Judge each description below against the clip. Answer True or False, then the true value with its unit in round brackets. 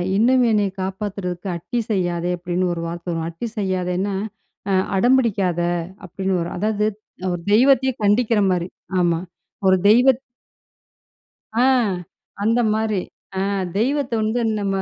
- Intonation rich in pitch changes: False (4.3 semitones)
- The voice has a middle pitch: False (200 Hz)